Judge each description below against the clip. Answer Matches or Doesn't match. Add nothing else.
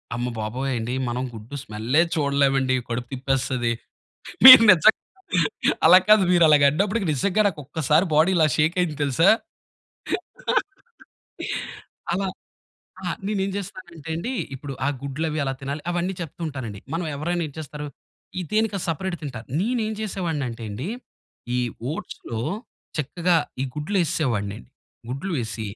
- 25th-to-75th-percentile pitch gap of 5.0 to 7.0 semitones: Matches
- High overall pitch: Doesn't match